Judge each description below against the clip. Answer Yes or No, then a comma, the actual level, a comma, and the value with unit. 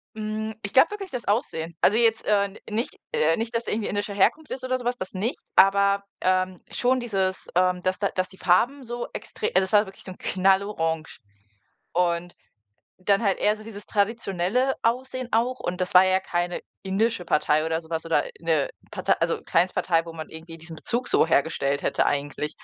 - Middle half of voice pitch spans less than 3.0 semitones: No, average, 4.5 semitones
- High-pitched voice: Yes, high, 195 Hz